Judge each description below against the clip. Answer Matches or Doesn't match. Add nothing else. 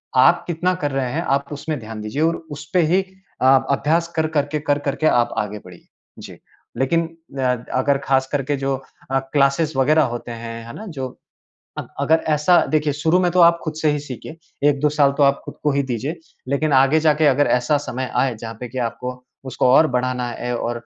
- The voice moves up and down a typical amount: Matches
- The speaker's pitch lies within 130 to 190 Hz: Matches